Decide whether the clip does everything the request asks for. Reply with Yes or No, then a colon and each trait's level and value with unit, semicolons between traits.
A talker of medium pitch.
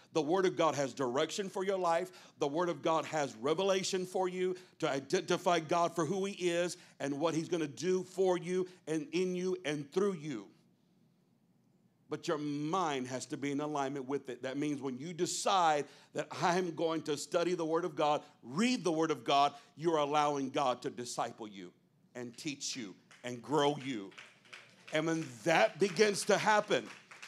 Yes: medium, 160 Hz